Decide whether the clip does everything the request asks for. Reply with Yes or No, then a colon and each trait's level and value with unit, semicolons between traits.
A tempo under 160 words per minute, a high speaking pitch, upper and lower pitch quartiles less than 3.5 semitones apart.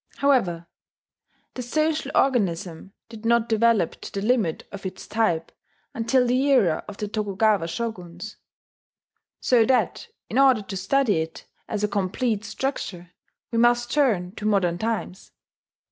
No: average, 140 wpm; high, 215 Hz; average, 4.4 semitones